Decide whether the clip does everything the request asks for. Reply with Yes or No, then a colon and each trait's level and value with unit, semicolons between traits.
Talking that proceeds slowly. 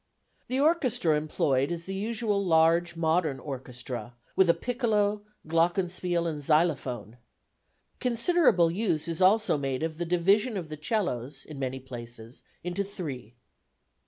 Yes: slow, 130 wpm